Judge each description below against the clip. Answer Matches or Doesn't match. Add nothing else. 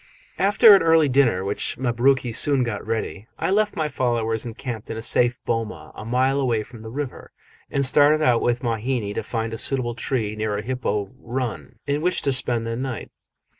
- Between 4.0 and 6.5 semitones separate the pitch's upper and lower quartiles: Doesn't match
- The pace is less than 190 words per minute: Doesn't match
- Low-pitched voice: Matches